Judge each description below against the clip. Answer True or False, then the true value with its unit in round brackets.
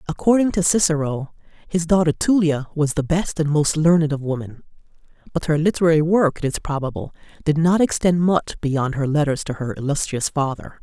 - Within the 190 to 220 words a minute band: False (175 wpm)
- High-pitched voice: False (155 Hz)